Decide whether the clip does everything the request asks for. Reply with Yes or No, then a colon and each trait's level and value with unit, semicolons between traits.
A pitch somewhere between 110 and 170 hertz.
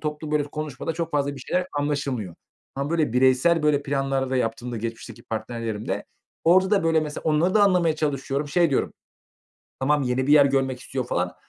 Yes: medium, 140 Hz